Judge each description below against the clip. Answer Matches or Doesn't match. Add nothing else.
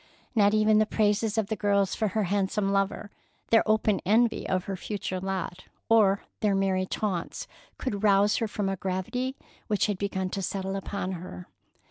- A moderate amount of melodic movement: Doesn't match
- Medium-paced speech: Matches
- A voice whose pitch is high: Matches